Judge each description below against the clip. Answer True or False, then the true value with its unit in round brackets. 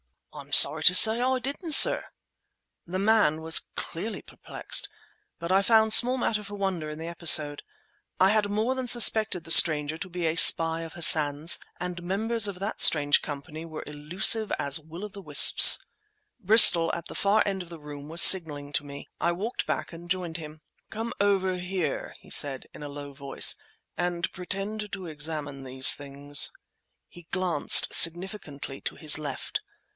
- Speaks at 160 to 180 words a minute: True (175 wpm)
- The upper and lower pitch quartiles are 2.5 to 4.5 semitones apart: False (5.0 semitones)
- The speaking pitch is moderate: True (170 Hz)